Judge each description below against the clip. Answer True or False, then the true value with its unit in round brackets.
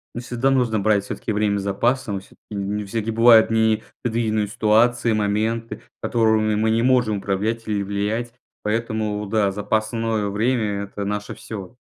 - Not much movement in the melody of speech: True (1.9 semitones)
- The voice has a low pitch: True (110 Hz)